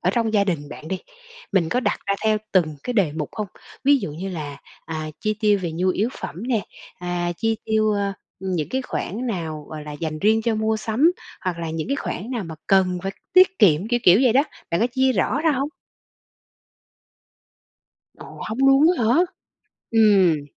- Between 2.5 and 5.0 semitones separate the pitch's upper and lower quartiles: No, wide, 5.4 semitones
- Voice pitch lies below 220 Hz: Yes, high, 200 Hz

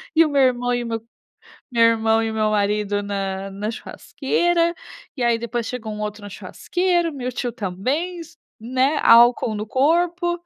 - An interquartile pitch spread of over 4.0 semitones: Yes, average, 5.2 semitones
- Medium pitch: No, high, 235 Hz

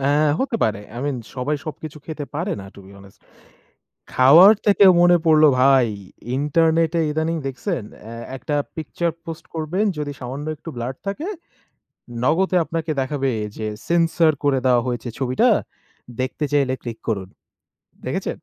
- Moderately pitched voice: Yes, medium, 150 Hz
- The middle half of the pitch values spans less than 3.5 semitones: No, average, 4.3 semitones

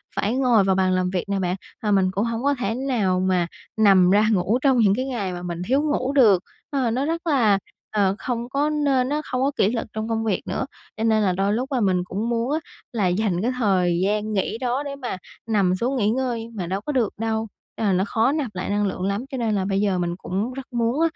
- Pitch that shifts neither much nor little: Yes, average, 4.7 semitones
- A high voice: Yes, high, 220 Hz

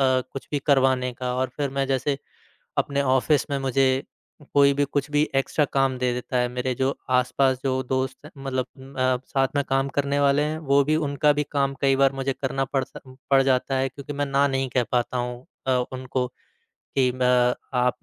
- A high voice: No, low, 135 Hz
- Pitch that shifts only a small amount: Yes, narrow, 1.5 semitones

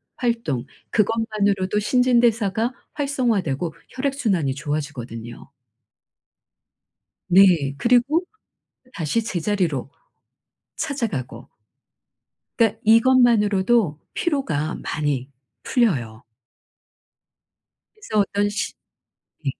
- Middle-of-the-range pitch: No, high, 205 Hz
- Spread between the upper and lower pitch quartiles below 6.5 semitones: No, wide, 7.9 semitones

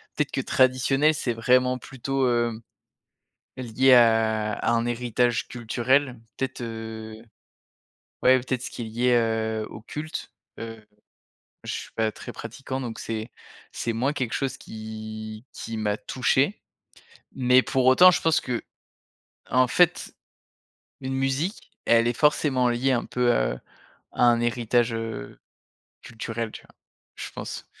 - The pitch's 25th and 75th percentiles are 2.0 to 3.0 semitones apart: Yes, narrow, 2.5 semitones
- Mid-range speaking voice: No, low, 120 Hz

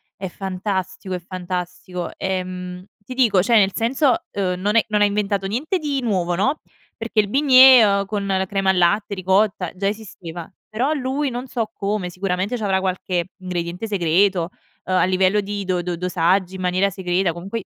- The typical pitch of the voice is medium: No, high, 195 Hz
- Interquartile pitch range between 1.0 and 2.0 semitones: No, average, 2.8 semitones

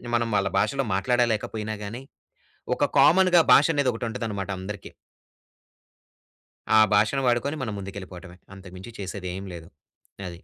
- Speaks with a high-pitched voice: No, low, 105 Hz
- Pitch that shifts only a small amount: No, average, 4.1 semitones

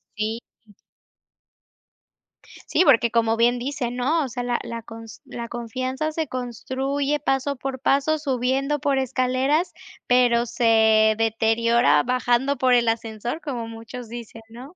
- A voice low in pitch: No, high, 245 Hz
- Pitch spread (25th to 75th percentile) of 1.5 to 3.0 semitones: Yes, average, 2.7 semitones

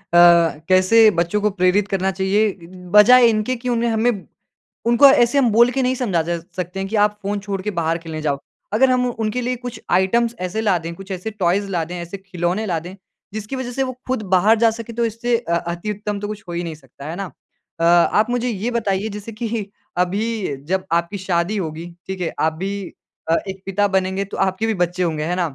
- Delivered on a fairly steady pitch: No, average, 4.3 semitones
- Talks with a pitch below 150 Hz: No, high, 200 Hz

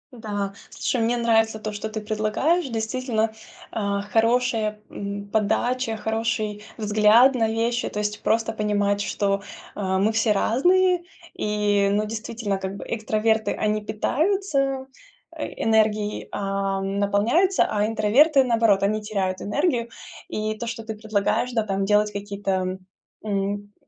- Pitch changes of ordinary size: No, narrow, 2.1 semitones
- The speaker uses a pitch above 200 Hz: Yes, high, 215 Hz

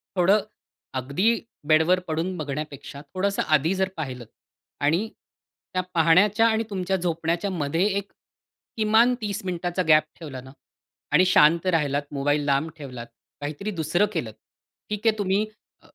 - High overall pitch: No, medium, 170 Hz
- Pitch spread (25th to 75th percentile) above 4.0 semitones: Yes, average, 4.8 semitones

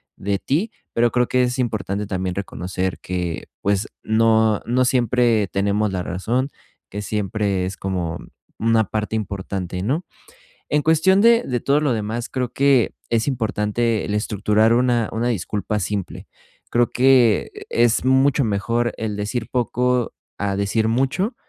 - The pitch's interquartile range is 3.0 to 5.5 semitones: Yes, average, 3.7 semitones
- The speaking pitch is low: Yes, low, 110 Hz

